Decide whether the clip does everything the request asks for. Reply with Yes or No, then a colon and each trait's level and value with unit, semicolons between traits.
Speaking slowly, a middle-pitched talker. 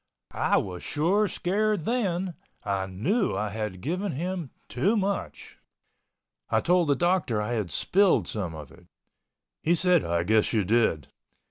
No: average, 150 wpm; medium, 155 Hz